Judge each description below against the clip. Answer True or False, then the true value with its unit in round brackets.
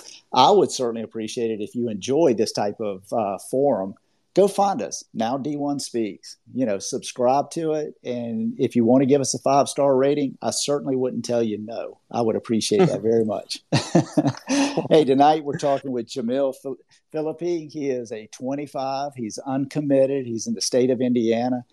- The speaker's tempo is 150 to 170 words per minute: False (180 wpm)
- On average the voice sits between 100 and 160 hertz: True (135 Hz)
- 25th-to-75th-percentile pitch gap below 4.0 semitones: True (3.5 semitones)